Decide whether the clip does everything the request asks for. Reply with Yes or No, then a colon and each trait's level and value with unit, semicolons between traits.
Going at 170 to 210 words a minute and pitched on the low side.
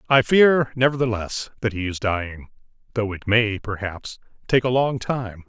No: average, 155 wpm; low, 115 Hz